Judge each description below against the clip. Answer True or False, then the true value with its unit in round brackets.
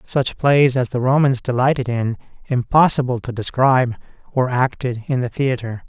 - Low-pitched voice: True (125 Hz)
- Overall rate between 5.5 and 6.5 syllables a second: False (5.1 syllables/s)